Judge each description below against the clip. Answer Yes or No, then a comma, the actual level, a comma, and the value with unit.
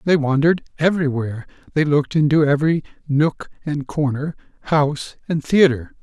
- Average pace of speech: No, slow, 130 wpm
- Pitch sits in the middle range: Yes, medium, 150 Hz